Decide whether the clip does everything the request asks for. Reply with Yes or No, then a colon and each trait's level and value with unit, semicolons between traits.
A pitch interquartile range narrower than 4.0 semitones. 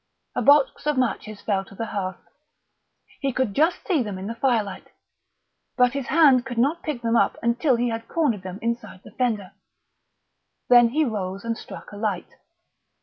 No: average, 4.3 semitones